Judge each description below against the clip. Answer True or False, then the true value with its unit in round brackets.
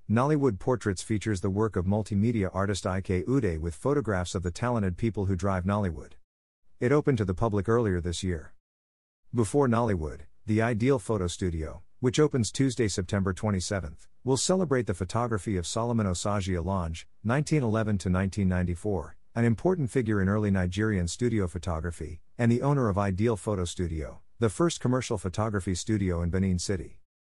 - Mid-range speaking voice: False (100 Hz)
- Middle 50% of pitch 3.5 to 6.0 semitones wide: True (4.4 semitones)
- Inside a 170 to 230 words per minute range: False (160 wpm)